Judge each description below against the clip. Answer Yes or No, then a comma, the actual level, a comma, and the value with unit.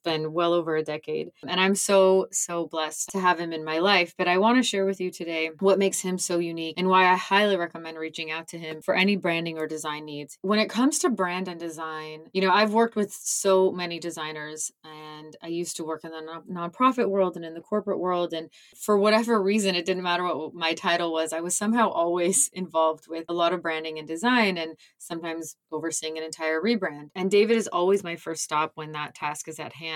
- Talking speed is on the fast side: Yes, fast, 230 wpm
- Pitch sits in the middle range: Yes, medium, 170 Hz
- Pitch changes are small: No, average, 3.1 semitones